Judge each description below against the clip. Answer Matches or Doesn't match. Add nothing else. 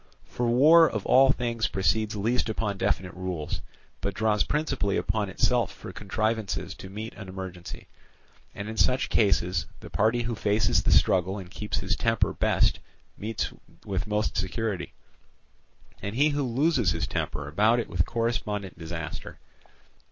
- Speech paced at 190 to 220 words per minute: Doesn't match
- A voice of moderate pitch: Doesn't match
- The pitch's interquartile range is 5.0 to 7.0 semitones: Doesn't match